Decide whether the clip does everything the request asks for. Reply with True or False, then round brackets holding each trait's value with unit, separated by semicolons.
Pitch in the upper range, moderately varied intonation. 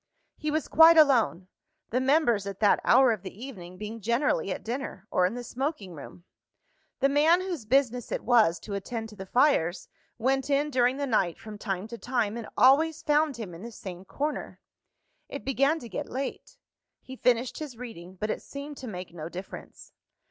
False (240 Hz; 5.7 semitones)